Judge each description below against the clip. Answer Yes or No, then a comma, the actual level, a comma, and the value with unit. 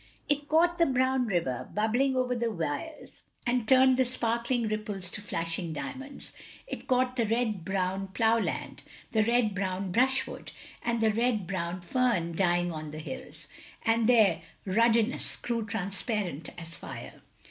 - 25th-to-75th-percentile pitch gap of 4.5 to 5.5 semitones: Yes, average, 5.2 semitones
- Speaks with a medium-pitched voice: No, high, 220 Hz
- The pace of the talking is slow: No, average, 155 wpm